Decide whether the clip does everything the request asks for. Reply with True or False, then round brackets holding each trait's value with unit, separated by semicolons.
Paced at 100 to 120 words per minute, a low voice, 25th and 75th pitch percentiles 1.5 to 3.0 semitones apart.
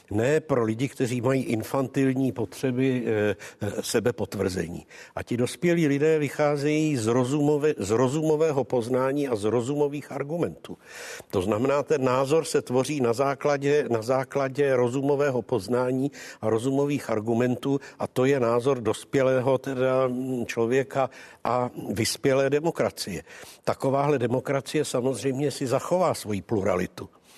True (115 wpm; 130 Hz; 2.6 semitones)